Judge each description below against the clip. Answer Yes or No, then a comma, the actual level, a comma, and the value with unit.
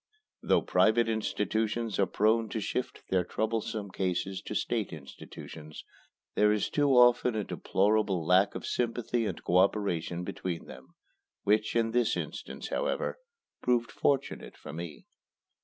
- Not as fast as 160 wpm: Yes, average, 140 wpm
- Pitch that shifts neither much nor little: Yes, average, 3.7 semitones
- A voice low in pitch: Yes, low, 105 Hz